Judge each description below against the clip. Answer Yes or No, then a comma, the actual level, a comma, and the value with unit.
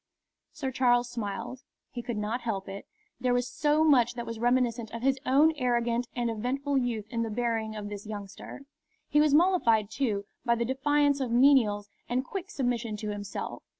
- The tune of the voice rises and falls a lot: No, average, 3.2 semitones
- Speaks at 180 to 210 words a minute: Yes, average, 185 wpm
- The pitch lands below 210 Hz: No, high, 240 Hz